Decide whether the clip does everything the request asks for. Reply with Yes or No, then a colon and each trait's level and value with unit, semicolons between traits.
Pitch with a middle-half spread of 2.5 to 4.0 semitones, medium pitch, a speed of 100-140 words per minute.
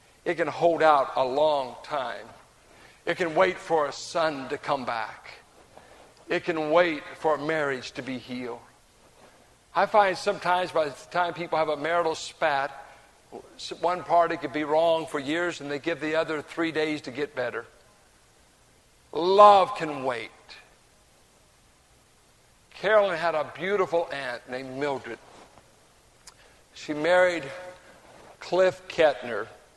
Yes: average, 3.5 semitones; medium, 160 Hz; slow, 135 wpm